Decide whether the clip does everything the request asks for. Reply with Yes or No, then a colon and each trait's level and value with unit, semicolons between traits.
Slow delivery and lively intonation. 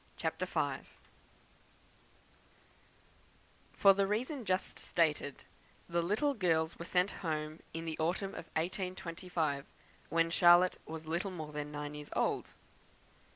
No: slow, 120 wpm; average, 2.9 semitones